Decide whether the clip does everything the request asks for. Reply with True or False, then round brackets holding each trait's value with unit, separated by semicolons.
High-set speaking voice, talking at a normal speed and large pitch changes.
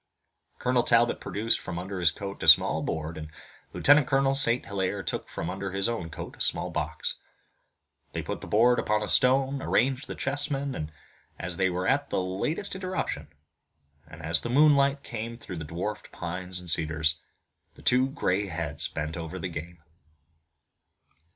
False (100 Hz; 170 wpm; 7.5 semitones)